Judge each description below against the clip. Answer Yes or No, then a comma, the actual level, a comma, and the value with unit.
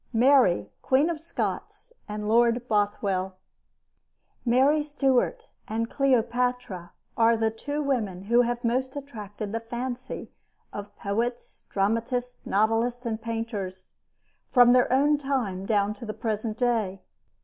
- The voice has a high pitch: Yes, high, 230 Hz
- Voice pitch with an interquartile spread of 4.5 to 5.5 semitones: No, average, 3.4 semitones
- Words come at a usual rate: No, slow, 125 wpm